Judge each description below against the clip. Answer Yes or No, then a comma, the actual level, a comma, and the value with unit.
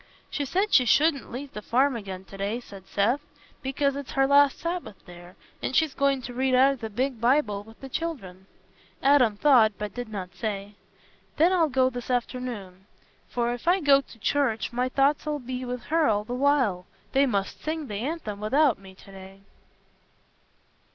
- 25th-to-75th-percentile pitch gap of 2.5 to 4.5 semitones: No, average, 5.2 semitones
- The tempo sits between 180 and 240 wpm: Yes, average, 185 wpm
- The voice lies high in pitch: Yes, very high, 250 Hz